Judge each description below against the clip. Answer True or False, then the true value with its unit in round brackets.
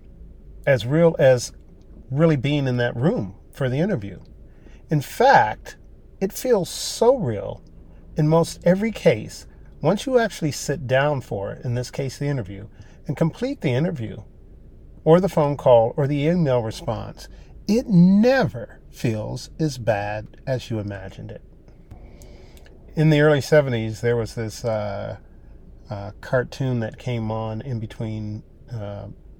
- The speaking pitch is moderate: False (120 Hz)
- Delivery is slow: False (145 wpm)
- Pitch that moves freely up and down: True (6.9 semitones)